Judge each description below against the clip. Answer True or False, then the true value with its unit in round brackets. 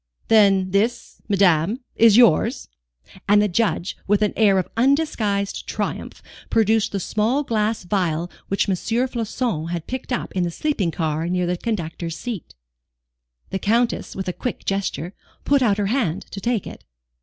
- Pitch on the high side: True (205 Hz)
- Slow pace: False (160 wpm)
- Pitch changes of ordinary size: True (4.2 semitones)